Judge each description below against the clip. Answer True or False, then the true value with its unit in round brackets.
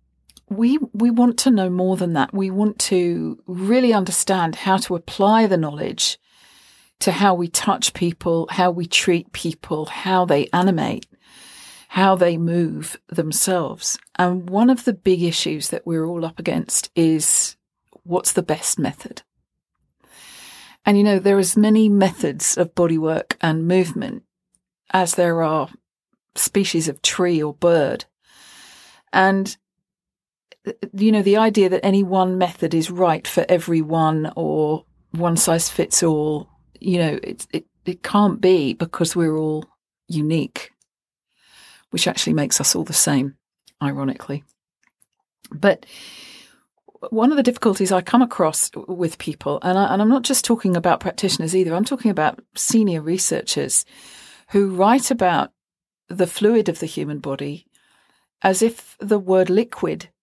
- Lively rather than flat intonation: False (3.2 semitones)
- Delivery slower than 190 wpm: True (145 wpm)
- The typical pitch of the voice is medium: True (180 Hz)